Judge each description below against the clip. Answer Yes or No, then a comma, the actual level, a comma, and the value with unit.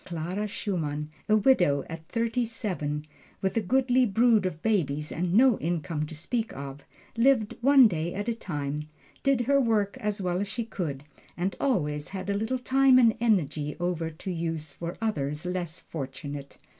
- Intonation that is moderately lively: No, wide, 6.7 semitones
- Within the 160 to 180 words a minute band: Yes, average, 170 wpm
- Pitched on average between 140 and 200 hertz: Yes, medium, 185 Hz